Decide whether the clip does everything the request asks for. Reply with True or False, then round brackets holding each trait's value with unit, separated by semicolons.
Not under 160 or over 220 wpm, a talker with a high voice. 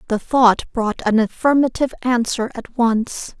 False (140 wpm; 240 Hz)